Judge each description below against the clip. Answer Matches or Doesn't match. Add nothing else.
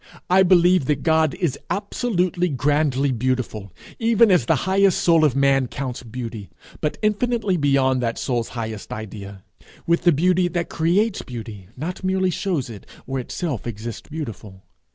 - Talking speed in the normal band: Matches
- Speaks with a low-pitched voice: Doesn't match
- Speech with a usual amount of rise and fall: Doesn't match